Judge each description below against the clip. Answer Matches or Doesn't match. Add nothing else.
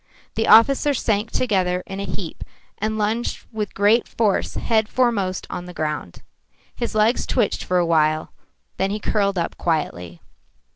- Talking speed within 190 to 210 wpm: Doesn't match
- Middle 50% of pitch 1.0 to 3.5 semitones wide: Doesn't match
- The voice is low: Doesn't match